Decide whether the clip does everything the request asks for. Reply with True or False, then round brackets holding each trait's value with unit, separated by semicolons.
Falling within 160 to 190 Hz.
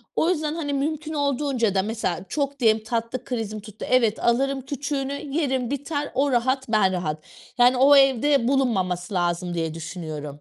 False (250 Hz)